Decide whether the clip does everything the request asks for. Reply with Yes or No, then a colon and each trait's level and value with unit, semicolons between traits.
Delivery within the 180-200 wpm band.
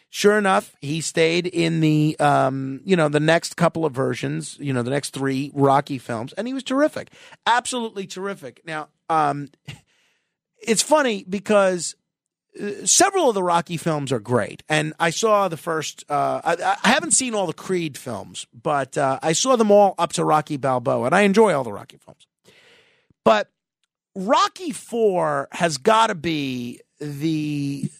No: average, 165 wpm